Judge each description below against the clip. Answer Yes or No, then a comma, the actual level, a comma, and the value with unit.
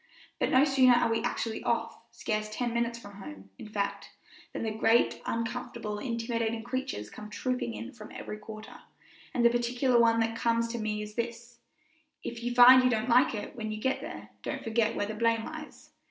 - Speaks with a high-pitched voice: Yes, high, 230 Hz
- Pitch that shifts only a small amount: Yes, narrow, 2.0 semitones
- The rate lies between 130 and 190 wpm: No, average, 200 wpm